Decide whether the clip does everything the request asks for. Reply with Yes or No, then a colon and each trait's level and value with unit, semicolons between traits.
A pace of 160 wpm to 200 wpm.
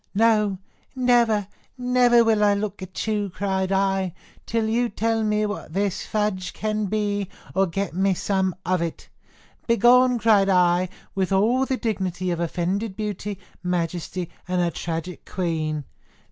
No: average, 145 wpm